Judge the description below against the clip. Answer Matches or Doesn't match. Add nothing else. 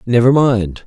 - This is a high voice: Doesn't match